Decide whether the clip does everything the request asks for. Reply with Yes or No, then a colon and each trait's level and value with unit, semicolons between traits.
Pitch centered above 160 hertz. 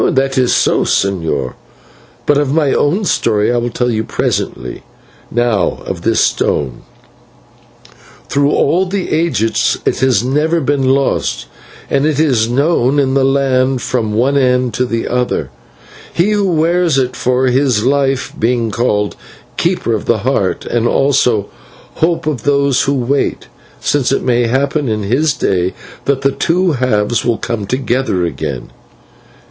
No: low, 130 Hz